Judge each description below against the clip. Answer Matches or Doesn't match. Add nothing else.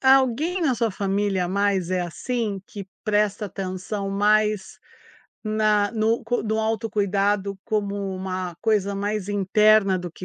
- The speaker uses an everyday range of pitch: Doesn't match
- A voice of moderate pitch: Doesn't match